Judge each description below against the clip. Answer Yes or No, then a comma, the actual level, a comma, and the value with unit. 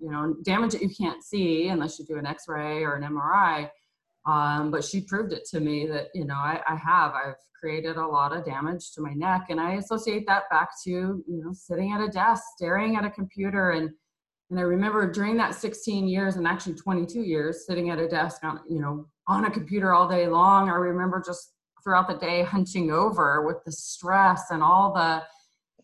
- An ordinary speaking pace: No, fast, 215 wpm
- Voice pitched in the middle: Yes, medium, 175 Hz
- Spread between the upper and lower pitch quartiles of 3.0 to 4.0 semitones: Yes, average, 3.5 semitones